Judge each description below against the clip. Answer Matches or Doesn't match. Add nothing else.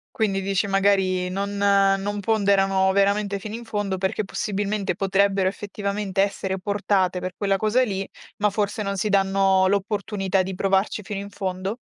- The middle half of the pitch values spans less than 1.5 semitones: Matches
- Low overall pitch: Doesn't match